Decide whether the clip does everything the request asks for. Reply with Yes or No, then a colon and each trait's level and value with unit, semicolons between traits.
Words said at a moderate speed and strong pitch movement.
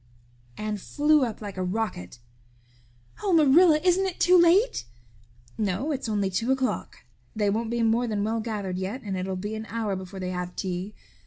Yes: average, 180 wpm; wide, 5.7 semitones